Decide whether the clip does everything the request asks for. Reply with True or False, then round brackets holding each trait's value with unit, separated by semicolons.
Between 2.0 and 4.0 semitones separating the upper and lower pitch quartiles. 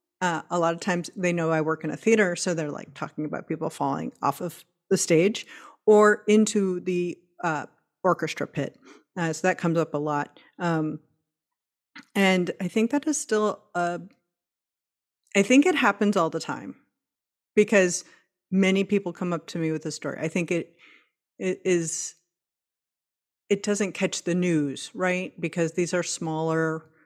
True (3.2 semitones)